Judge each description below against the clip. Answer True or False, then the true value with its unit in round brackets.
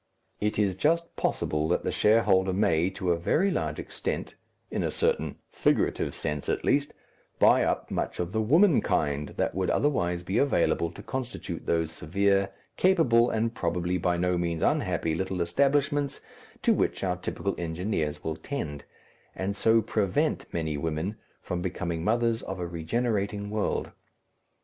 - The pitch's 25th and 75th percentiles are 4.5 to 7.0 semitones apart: True (5.3 semitones)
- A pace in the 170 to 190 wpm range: False (155 wpm)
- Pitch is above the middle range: False (95 Hz)